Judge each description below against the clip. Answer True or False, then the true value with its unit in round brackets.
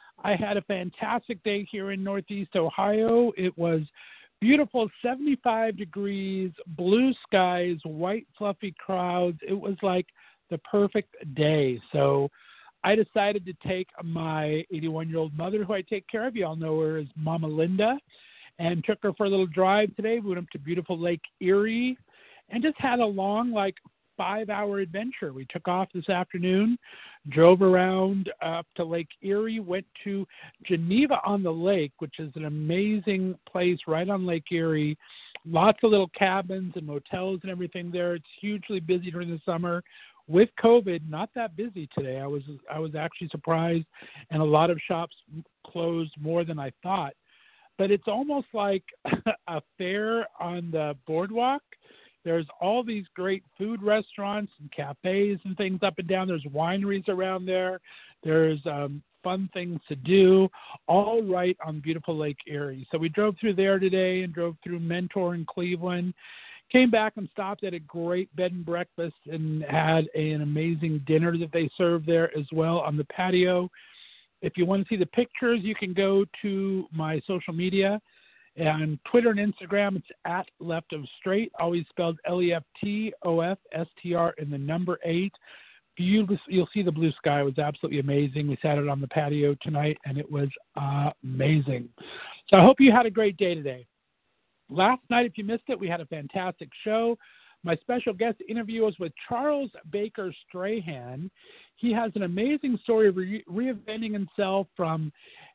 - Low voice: False (180 Hz)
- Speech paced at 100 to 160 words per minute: False (170 wpm)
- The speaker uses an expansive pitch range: False (4.0 semitones)